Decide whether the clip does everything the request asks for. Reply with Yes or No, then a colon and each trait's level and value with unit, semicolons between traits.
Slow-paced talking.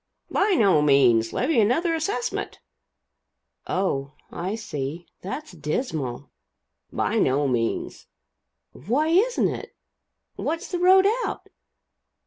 Yes: slow, 105 wpm